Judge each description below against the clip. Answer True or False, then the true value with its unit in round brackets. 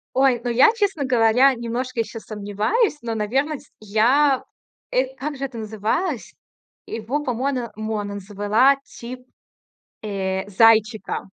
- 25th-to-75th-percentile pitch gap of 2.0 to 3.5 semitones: False (3.9 semitones)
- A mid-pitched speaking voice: False (235 Hz)